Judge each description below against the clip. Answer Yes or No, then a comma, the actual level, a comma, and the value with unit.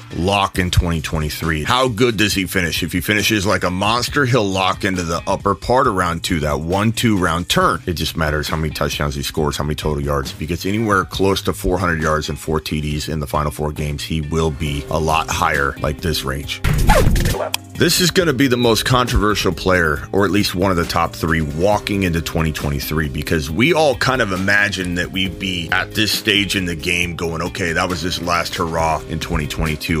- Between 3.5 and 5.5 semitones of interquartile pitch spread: Yes, average, 4.1 semitones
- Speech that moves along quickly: Yes, fast, 210 wpm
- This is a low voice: Yes, very low, 90 Hz